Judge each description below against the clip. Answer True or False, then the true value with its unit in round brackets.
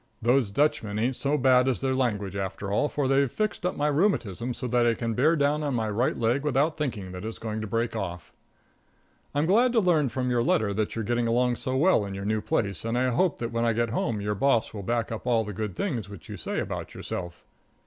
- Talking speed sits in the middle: False (245 wpm)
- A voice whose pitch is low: True (120 Hz)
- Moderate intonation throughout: True (4.3 semitones)